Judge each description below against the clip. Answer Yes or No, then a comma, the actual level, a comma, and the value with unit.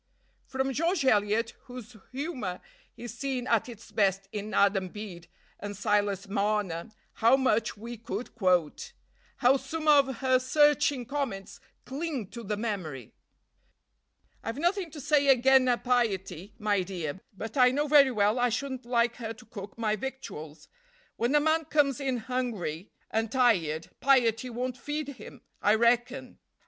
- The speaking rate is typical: Yes, average, 150 wpm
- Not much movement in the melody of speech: No, average, 4.4 semitones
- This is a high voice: Yes, high, 240 Hz